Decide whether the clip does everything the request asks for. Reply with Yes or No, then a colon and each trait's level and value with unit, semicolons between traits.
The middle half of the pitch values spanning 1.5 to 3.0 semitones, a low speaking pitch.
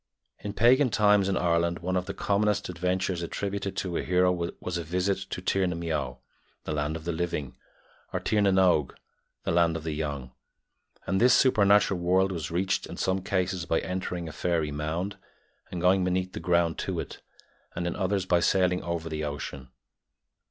Yes: narrow, 2.5 semitones; very low, 90 Hz